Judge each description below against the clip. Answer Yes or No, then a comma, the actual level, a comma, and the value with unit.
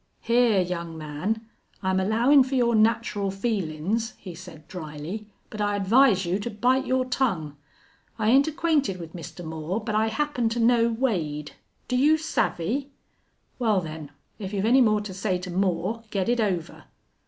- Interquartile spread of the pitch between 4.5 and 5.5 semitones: Yes, average, 4.9 semitones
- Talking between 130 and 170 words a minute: Yes, average, 165 wpm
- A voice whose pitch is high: Yes, high, 210 Hz